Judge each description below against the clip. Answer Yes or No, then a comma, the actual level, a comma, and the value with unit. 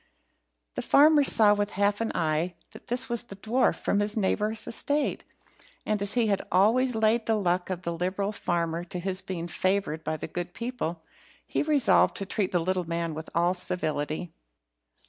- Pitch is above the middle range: Yes, high, 195 Hz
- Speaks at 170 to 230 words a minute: Yes, average, 185 wpm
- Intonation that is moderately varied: Yes, average, 4.2 semitones